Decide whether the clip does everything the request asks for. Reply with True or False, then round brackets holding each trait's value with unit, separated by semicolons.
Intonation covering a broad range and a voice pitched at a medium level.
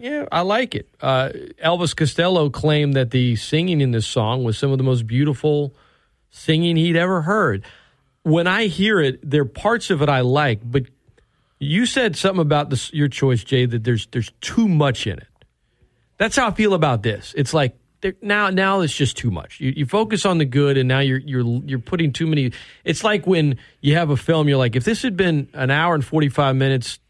False (4.9 semitones; 145 Hz)